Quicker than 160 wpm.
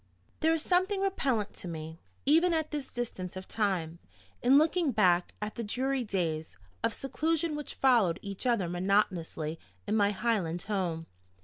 No: average, 155 wpm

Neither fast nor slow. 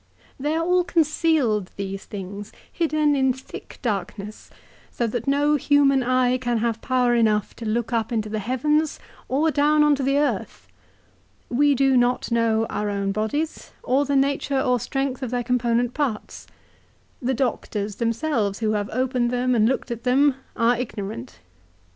Yes: average, 165 wpm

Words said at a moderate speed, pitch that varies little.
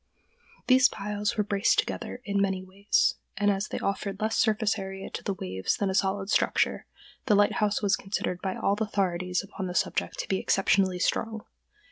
Yes: average, 175 wpm; narrow, 1.5 semitones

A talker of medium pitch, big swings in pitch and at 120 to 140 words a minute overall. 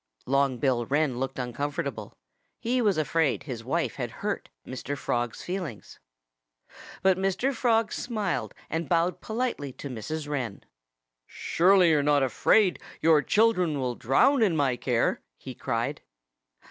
Yes: medium, 155 Hz; wide, 6.5 semitones; slow, 135 wpm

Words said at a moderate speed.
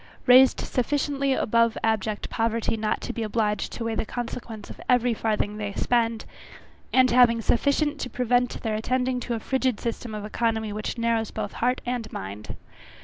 Yes: average, 170 wpm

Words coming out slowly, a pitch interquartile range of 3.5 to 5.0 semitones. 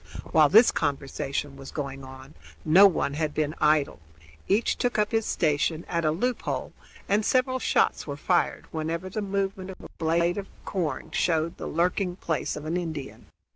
No: average, 175 wpm; average, 4.3 semitones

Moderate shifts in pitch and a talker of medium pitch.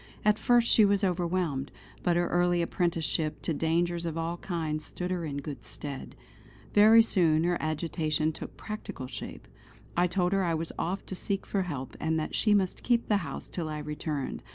Yes: average, 3.1 semitones; medium, 170 Hz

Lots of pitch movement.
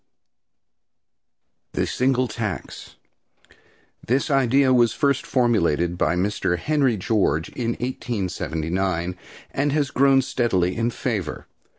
Yes: wide, 6.4 semitones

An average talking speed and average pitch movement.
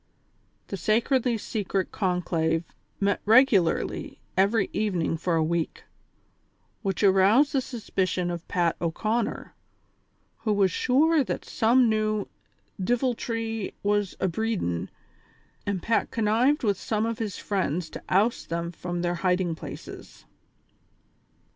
No: slow, 115 wpm; average, 4.3 semitones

